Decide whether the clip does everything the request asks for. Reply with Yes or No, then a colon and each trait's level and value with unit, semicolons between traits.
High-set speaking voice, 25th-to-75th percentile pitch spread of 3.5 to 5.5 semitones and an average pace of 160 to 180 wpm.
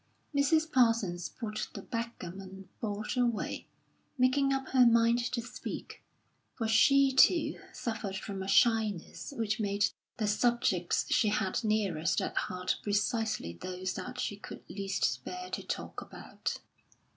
No: high, 220 Hz; average, 4.0 semitones; slow, 135 wpm